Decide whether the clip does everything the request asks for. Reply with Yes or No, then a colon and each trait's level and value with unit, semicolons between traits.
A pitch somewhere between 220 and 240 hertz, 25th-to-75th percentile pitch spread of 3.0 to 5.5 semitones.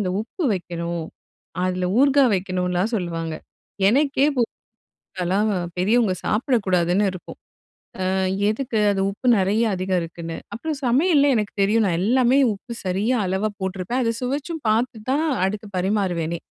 No: high, 205 Hz; average, 5.2 semitones